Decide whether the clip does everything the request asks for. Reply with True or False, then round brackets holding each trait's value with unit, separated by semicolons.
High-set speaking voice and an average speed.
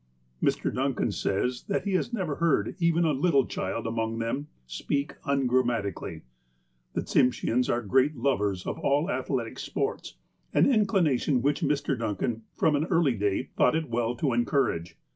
False (130 Hz; 155 wpm)